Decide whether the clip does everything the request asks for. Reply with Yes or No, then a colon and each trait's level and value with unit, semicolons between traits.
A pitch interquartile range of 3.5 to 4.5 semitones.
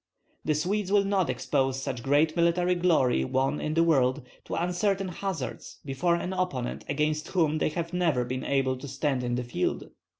No: average, 5.1 semitones